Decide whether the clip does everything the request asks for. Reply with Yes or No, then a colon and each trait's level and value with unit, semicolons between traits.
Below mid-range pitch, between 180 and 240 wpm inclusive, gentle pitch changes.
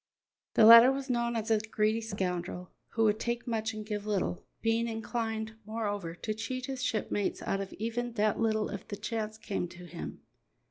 No: high, 220 Hz; average, 185 wpm; narrow, 1.8 semitones